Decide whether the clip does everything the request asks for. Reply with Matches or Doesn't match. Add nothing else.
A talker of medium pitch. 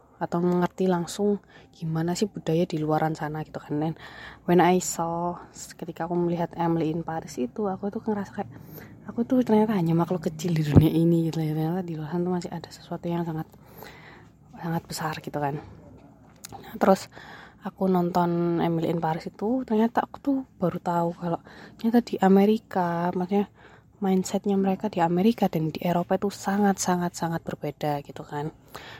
Matches